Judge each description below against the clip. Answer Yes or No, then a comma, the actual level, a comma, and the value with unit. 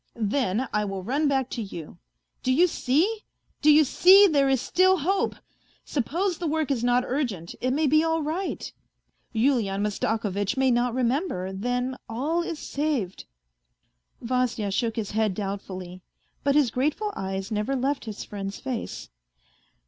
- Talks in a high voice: Yes, very high, 255 Hz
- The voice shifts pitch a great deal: Yes, wide, 6.2 semitones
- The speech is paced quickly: No, average, 155 wpm